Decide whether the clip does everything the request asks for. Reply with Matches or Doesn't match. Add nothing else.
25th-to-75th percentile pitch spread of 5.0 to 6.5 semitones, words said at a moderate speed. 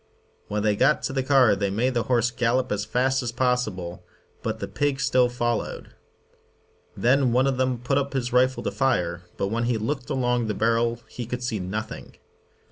Doesn't match